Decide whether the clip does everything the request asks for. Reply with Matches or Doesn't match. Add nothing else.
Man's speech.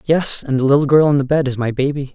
Matches